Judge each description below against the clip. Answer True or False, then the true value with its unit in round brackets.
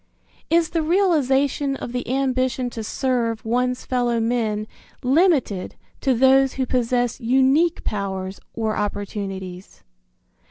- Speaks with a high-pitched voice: True (250 Hz)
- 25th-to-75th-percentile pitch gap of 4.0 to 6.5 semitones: False (3.3 semitones)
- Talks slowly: True (115 wpm)